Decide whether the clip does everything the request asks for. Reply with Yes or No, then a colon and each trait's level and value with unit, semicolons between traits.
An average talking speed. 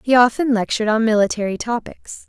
Yes: average, 160 wpm